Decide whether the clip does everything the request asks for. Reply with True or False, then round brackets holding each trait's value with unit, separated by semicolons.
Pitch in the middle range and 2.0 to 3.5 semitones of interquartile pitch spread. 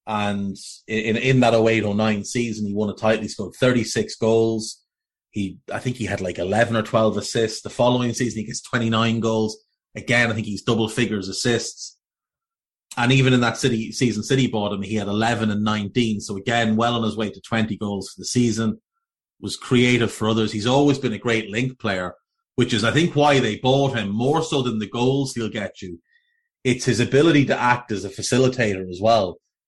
False (115 Hz; 2.9 semitones)